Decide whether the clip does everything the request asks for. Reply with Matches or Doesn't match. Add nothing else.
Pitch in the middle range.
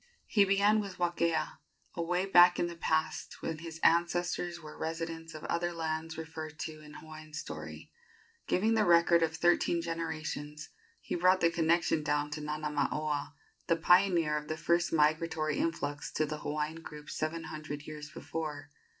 Matches